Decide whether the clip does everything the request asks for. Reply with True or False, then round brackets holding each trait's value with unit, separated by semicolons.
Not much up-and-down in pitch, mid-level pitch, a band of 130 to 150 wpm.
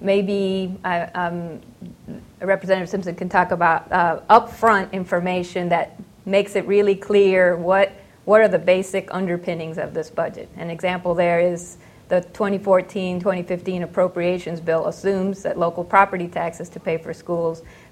True (2.2 semitones; 180 Hz; 135 wpm)